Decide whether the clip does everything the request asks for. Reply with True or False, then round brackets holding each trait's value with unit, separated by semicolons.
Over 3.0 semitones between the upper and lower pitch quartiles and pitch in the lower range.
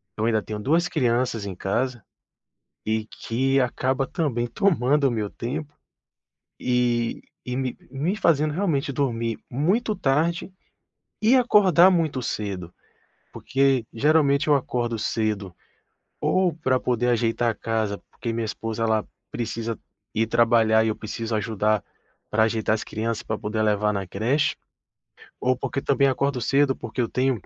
True (4.1 semitones; 120 Hz)